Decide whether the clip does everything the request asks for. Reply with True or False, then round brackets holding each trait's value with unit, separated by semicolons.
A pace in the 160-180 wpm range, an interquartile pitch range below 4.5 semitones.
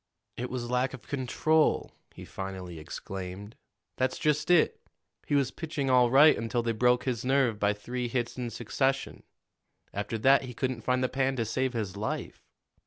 True (175 wpm; 3.0 semitones)